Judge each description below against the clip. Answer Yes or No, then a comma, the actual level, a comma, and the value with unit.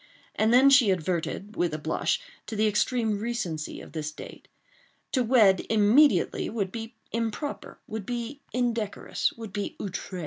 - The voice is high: Yes, high, 220 Hz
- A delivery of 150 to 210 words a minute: No, average, 140 wpm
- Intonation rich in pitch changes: No, average, 3.8 semitones